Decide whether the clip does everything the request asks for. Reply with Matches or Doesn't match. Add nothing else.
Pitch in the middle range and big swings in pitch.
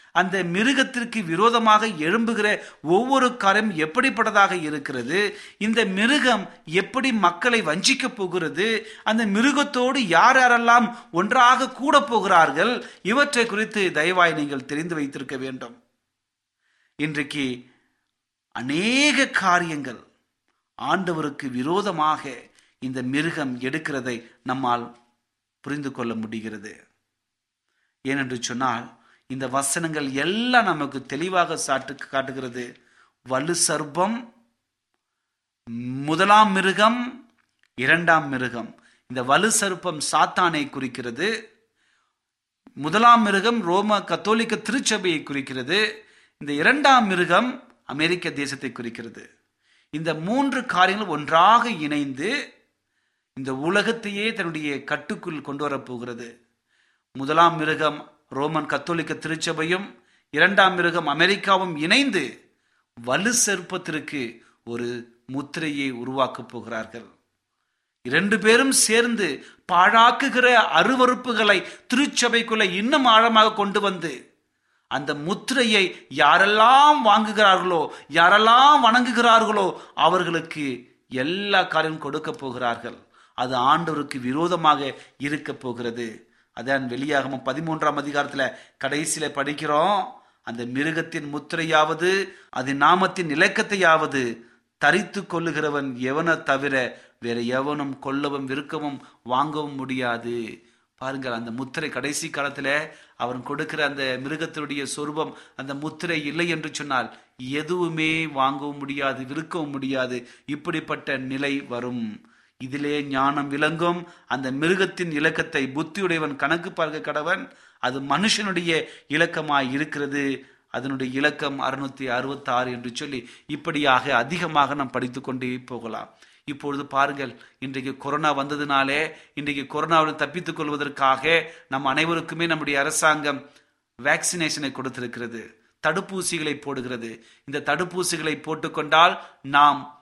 Matches